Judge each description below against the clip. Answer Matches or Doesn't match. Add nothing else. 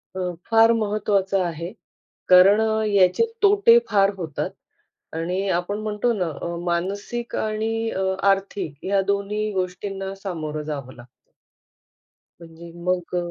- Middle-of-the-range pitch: Doesn't match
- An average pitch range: Matches